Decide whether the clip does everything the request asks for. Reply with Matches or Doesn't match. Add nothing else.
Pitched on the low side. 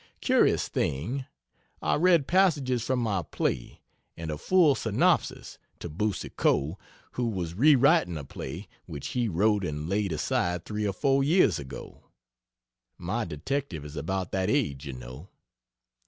Matches